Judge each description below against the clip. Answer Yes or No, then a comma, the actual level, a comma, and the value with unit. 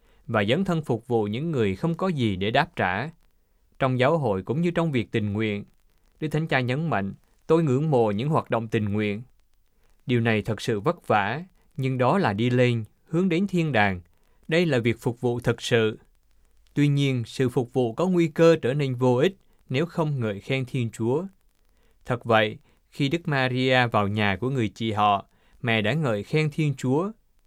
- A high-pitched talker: No, low, 125 Hz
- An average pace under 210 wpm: Yes, average, 200 wpm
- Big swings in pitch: Yes, wide, 6.0 semitones